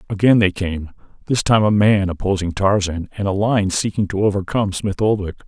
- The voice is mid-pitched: No, low, 100 Hz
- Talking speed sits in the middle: Yes, average, 185 wpm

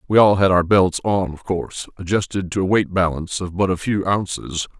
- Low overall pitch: Yes, very low, 95 Hz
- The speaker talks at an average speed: No, fast, 225 wpm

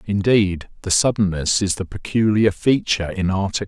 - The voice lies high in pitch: No, low, 100 Hz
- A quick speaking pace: No, average, 145 wpm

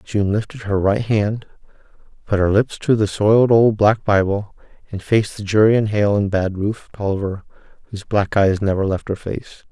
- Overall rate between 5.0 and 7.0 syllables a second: Yes, 5.3 syllables/s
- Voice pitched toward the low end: Yes, low, 105 Hz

